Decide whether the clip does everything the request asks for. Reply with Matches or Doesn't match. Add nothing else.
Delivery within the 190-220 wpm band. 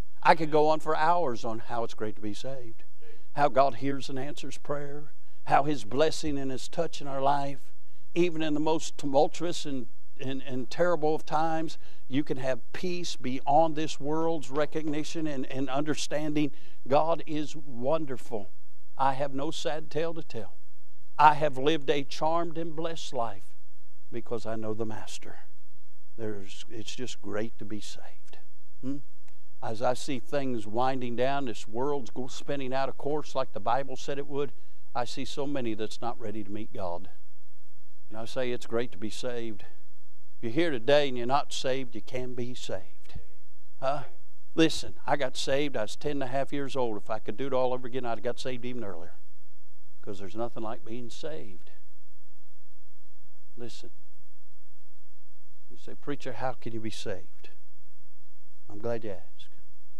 Doesn't match